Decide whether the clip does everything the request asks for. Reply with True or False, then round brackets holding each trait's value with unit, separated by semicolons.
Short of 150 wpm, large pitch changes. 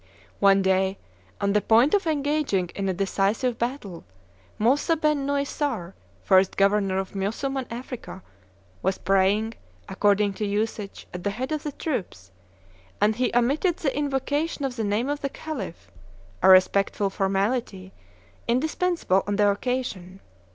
True (135 wpm; 5.9 semitones)